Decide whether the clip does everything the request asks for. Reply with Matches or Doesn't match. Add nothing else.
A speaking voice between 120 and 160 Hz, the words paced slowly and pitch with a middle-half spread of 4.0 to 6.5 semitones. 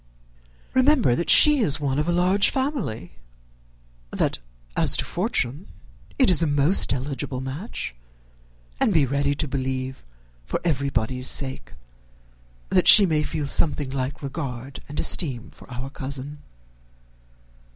Matches